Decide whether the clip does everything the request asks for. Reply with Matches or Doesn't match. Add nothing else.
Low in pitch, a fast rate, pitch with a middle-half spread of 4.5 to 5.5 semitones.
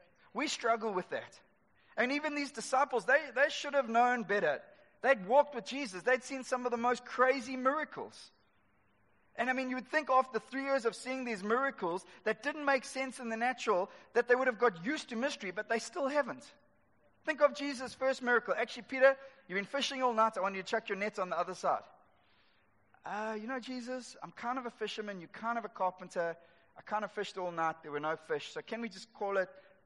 Doesn't match